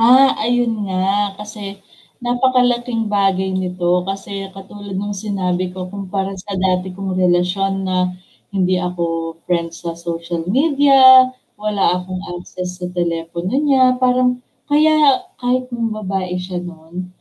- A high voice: Yes, high, 195 Hz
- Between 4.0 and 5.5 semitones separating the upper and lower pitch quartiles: Yes, average, 4.6 semitones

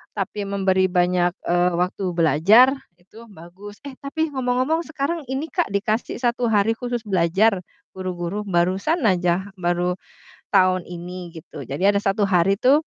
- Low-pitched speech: No, high, 195 Hz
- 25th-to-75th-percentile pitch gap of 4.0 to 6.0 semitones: Yes, average, 5.0 semitones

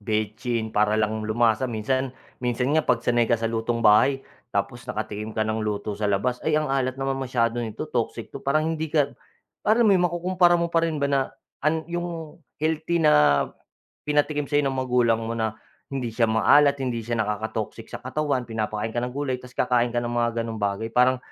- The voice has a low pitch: Yes, low, 120 Hz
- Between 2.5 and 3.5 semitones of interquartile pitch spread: No, average, 4.7 semitones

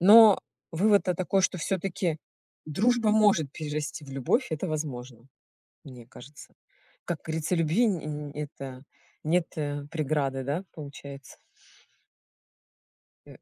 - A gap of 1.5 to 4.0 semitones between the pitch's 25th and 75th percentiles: No, average, 4.6 semitones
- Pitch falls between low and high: Yes, medium, 155 Hz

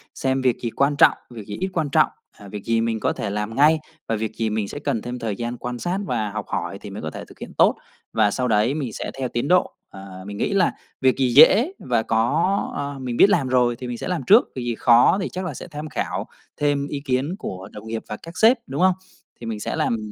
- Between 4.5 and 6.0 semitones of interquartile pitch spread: Yes, average, 4.8 semitones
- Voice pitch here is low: Yes, low, 125 Hz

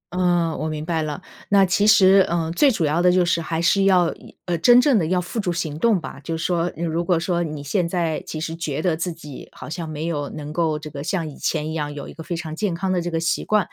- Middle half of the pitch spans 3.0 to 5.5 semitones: No, narrow, 2.5 semitones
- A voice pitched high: No, medium, 170 Hz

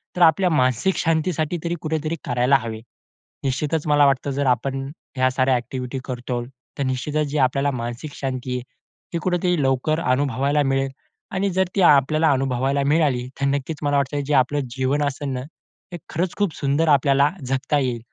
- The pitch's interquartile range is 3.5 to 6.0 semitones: No, average, 3.0 semitones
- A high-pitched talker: No, medium, 140 Hz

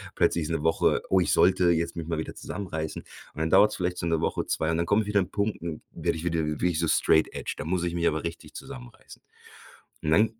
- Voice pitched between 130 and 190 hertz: No, very low, 85 Hz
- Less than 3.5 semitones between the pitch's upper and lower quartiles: Yes, average, 2.9 semitones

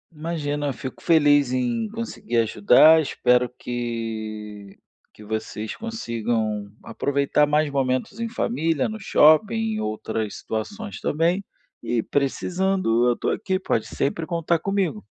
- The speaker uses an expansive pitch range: Yes, wide, 6.7 semitones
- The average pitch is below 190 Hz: Yes, medium, 140 Hz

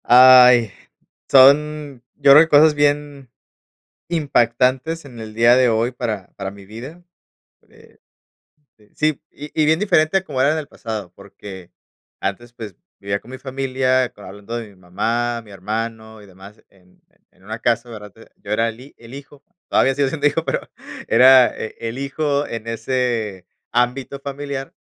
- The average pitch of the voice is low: Yes, low, 125 Hz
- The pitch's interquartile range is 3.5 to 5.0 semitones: Yes, average, 4.2 semitones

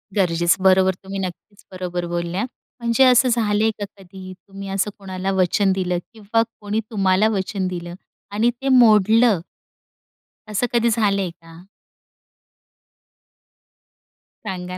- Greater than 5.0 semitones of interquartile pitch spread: No, average, 2.7 semitones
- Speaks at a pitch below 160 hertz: No, high, 195 Hz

